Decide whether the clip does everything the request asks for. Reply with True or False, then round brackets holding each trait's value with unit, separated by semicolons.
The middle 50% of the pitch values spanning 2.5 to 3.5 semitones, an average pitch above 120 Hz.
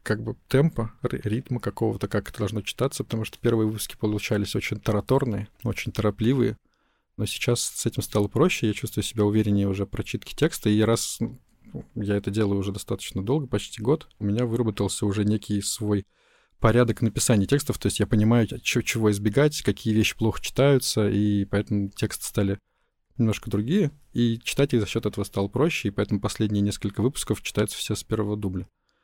False (2.9 semitones; 110 Hz)